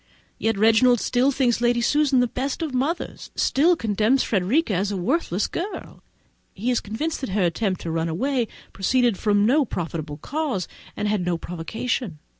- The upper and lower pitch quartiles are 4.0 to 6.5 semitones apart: Yes, wide, 5.5 semitones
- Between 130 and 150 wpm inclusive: No, average, 175 wpm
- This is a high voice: Yes, high, 230 Hz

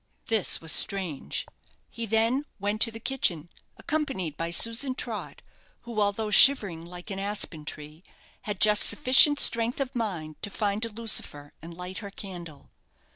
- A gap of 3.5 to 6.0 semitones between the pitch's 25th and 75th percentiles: Yes, average, 5.0 semitones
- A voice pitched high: Yes, high, 205 Hz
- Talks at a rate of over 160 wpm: No, average, 155 wpm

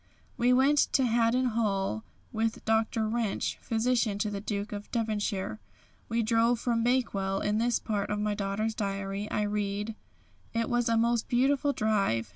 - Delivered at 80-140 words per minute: No, average, 160 wpm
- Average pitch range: No, narrow, 2.3 semitones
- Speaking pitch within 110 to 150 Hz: No, high, 220 Hz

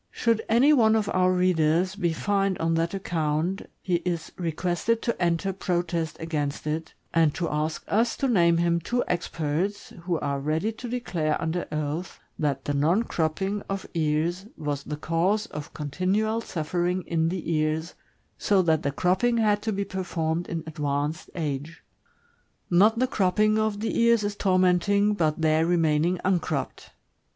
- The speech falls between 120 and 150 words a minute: No, average, 160 wpm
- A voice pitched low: No, medium, 175 Hz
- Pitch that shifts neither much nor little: Yes, average, 4.1 semitones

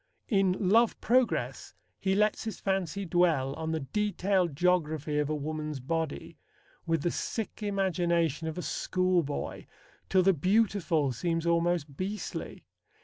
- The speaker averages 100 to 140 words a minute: Yes, slow, 135 wpm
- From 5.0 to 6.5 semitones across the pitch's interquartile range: No, average, 3.9 semitones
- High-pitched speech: No, medium, 175 Hz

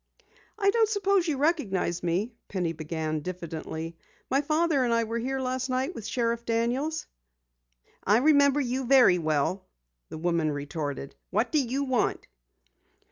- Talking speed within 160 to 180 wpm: No, average, 145 wpm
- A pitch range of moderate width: No, wide, 8.6 semitones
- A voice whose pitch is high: Yes, high, 235 Hz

